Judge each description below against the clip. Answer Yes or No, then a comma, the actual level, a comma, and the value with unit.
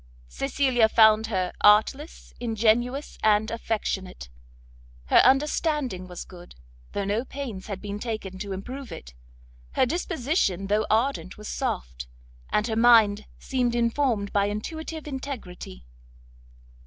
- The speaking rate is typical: No, slow, 120 wpm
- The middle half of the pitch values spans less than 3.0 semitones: No, average, 4.7 semitones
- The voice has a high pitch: Yes, high, 220 Hz